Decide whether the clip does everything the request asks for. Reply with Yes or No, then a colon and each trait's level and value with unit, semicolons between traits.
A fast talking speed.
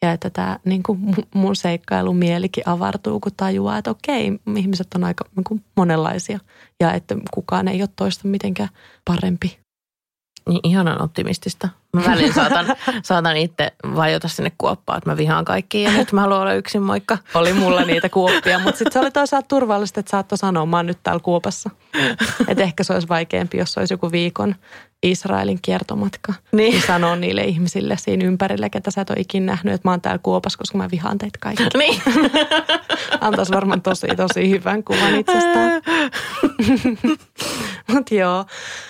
Yes: fast, 170 wpm